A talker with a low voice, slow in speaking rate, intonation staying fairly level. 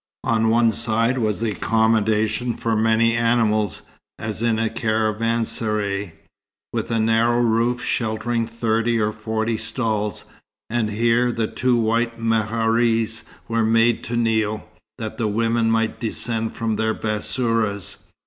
Yes: low, 115 Hz; slow, 130 wpm; narrow, 1.0 semitones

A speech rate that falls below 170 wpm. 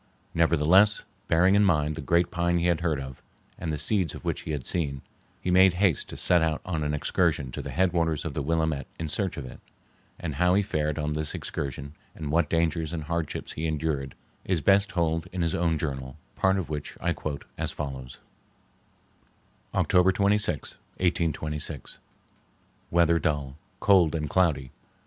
No: average, 175 wpm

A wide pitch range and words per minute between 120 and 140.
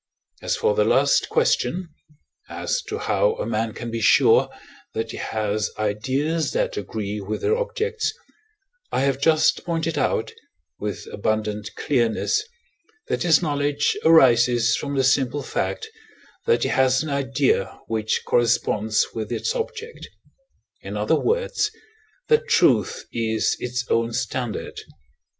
Yes: wide, 7.9 semitones; slow, 135 wpm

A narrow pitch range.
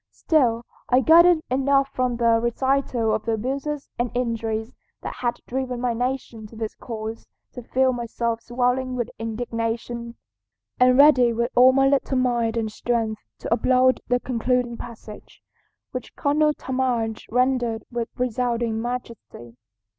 Yes: narrow, 2.0 semitones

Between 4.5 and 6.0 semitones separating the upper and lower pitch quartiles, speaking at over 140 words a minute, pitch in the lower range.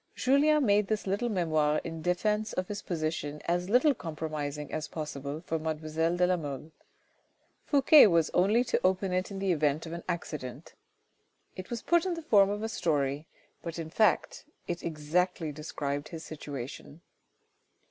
No: average, 4.8 semitones; average, 165 wpm; medium, 170 Hz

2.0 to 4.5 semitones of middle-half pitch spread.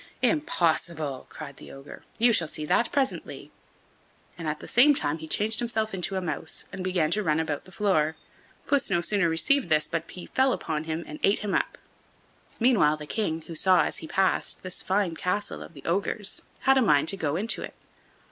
No: average, 5.1 semitones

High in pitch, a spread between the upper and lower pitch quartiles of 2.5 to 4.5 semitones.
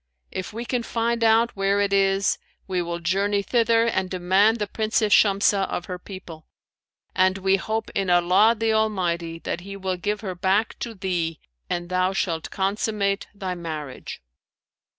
Yes: high, 195 Hz; average, 2.9 semitones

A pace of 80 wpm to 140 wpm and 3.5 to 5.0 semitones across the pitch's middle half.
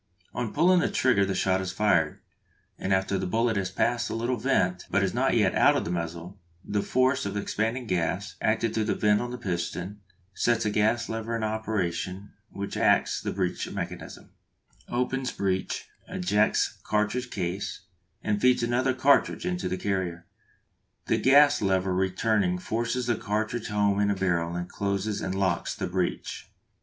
No: average, 175 wpm; average, 3.9 semitones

